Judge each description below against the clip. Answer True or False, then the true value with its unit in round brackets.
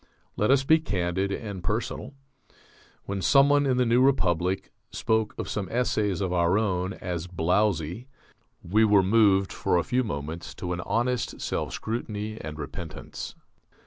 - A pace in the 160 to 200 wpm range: False (150 wpm)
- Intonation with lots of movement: False (4.5 semitones)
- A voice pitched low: True (100 Hz)